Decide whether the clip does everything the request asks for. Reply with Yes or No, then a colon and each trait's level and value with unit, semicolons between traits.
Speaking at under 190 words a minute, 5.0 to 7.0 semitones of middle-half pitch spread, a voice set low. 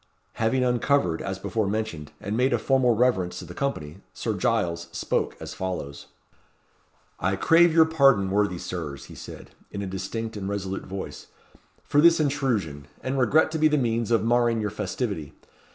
Yes: average, 170 wpm; wide, 5.6 semitones; low, 110 Hz